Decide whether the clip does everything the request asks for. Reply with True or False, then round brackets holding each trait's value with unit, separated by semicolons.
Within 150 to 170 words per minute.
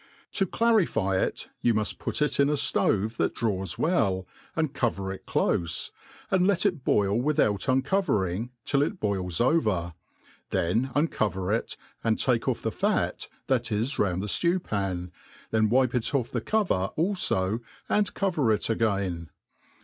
True (160 wpm)